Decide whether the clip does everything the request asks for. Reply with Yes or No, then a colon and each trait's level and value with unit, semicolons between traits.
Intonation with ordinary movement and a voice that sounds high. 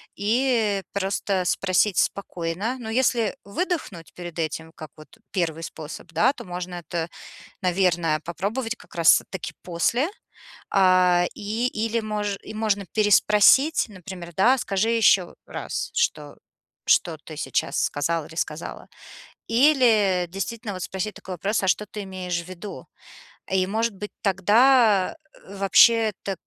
Yes: average, 3.8 semitones; high, 195 Hz